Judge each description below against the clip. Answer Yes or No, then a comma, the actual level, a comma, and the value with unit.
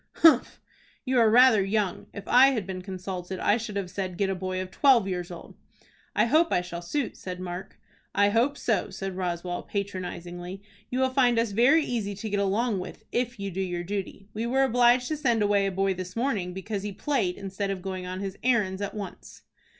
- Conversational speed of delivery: No, fast, 210 wpm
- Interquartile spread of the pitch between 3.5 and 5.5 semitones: Yes, average, 4.2 semitones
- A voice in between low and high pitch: No, high, 200 Hz